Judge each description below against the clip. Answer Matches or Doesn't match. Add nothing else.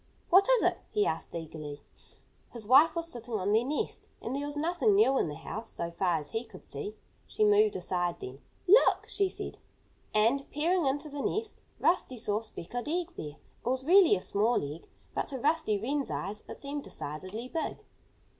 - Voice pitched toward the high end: Matches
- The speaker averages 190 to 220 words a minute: Matches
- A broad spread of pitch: Matches